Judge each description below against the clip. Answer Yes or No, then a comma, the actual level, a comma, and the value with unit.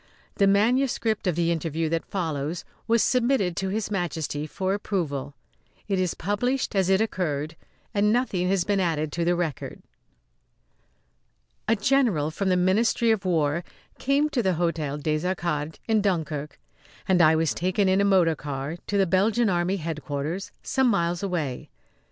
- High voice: No, medium, 180 Hz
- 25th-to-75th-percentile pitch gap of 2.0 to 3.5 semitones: No, average, 4.2 semitones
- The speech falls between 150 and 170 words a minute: Yes, average, 160 wpm